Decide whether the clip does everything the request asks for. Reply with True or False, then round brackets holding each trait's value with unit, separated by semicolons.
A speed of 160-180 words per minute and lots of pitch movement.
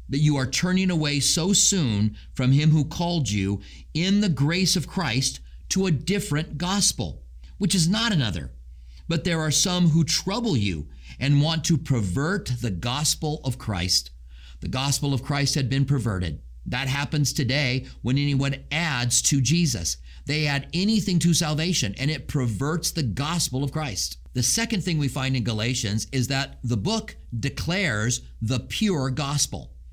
True (165 wpm; 6.2 semitones)